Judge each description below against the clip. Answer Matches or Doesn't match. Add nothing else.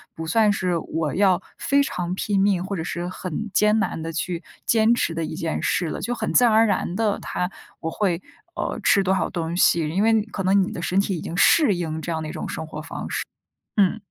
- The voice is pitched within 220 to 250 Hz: Doesn't match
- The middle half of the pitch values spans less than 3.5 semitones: Doesn't match